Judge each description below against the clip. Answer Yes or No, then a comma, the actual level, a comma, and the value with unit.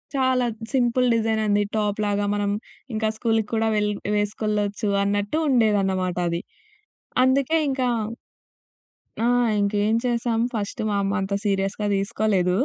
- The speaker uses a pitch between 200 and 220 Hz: Yes, high, 210 Hz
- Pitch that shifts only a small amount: Yes, narrow, 2.2 semitones